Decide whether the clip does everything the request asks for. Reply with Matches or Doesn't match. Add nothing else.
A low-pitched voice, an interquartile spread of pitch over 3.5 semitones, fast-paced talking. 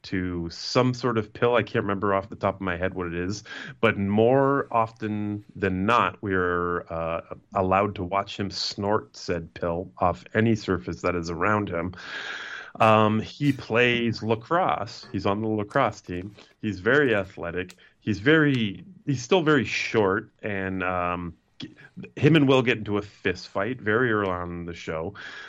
Doesn't match